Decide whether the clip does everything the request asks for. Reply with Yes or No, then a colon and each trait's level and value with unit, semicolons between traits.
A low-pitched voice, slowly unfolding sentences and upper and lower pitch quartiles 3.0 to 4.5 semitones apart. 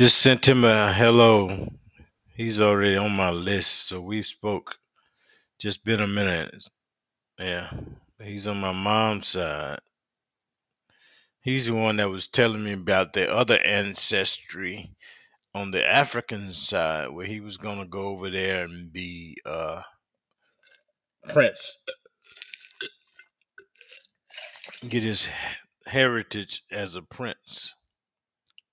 Yes: low, 105 Hz; slow, 115 wpm; average, 4.0 semitones